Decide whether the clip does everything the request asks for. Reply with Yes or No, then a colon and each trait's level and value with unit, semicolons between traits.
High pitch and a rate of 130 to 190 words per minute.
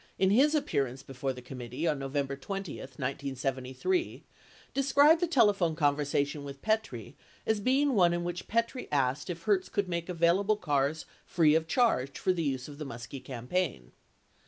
No: medium, 160 Hz; average, 160 wpm